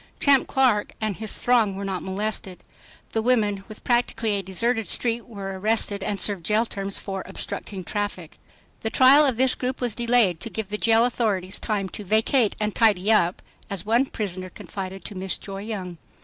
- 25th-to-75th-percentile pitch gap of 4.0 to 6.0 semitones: No, average, 3.0 semitones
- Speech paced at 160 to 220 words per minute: Yes, average, 185 wpm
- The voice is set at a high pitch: Yes, high, 210 Hz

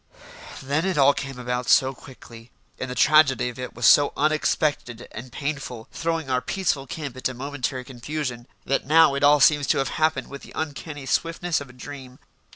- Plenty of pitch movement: No, average, 3.2 semitones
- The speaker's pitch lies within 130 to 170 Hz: Yes, medium, 140 Hz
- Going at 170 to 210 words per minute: Yes, average, 185 wpm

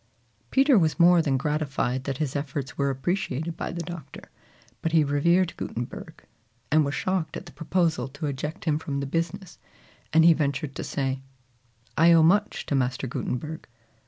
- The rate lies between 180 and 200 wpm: No, average, 170 wpm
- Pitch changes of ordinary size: Yes, average, 3.4 semitones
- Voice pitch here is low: No, medium, 155 Hz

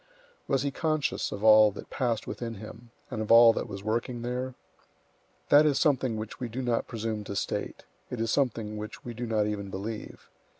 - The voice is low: Yes, low, 115 Hz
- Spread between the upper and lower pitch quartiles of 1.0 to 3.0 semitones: Yes, average, 2.7 semitones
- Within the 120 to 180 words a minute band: No, average, 200 wpm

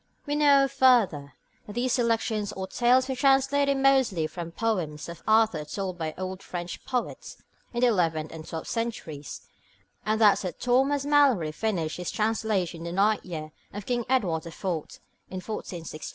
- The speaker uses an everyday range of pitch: No, wide, 6.8 semitones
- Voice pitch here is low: No, high, 210 Hz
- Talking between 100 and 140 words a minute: No, average, 165 wpm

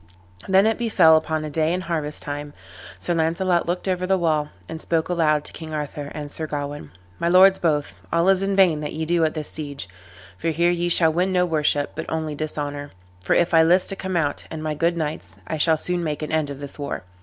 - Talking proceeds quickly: Yes, fast, 235 wpm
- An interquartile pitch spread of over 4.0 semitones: No, narrow, 2.6 semitones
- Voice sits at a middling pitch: Yes, medium, 160 Hz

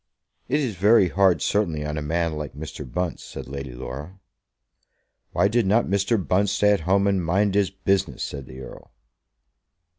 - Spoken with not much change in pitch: No, average, 4.9 semitones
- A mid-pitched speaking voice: No, very low, 95 Hz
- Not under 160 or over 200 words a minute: Yes, average, 175 wpm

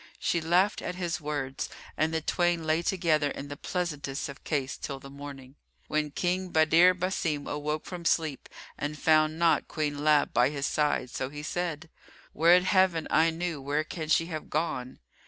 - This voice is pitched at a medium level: Yes, medium, 155 Hz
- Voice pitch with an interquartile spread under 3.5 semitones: Yes, average, 2.8 semitones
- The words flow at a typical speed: Yes, average, 175 wpm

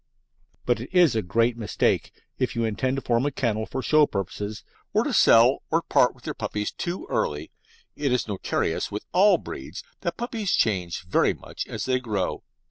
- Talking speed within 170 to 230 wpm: Yes, average, 185 wpm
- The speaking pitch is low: Yes, low, 115 Hz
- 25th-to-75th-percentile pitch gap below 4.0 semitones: No, average, 4.6 semitones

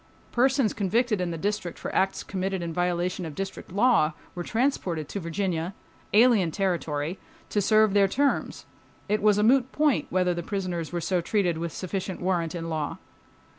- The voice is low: No, high, 190 Hz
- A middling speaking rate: Yes, average, 160 wpm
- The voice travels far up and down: No, average, 3.6 semitones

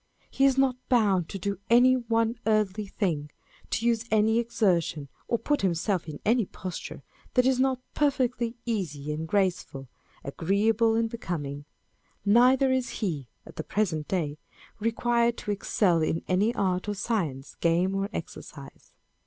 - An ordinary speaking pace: Yes, average, 150 wpm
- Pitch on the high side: Yes, high, 205 Hz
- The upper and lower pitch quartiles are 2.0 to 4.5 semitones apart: No, average, 5.3 semitones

